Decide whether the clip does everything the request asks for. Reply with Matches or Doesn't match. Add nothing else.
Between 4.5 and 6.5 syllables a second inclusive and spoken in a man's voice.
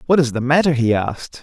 Matches